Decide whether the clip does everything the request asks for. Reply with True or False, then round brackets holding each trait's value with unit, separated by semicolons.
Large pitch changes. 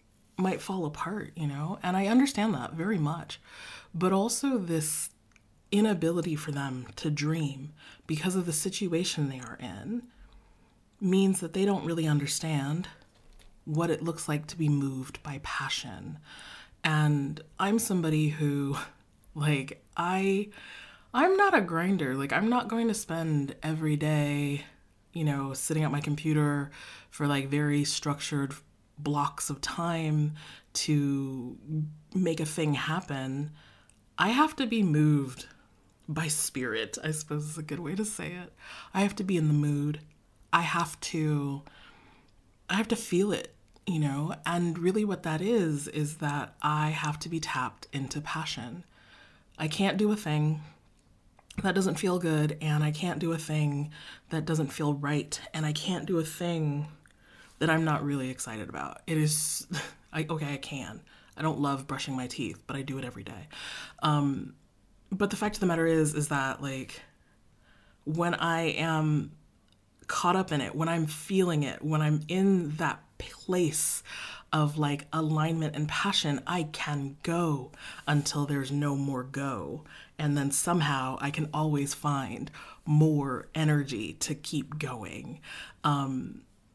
False (3.0 semitones)